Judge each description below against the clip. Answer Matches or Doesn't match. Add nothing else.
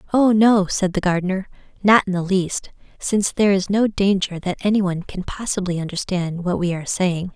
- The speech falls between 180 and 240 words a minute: Matches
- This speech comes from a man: Doesn't match